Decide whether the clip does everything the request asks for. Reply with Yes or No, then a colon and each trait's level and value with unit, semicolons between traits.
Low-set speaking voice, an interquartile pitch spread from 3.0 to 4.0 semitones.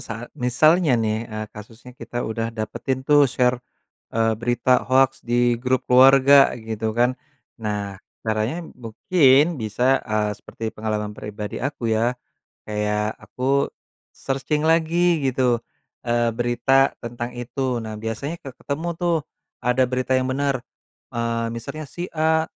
Yes: low, 125 Hz; average, 3.3 semitones